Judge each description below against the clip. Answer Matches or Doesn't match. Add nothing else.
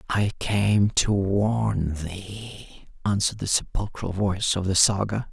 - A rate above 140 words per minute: Doesn't match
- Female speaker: Doesn't match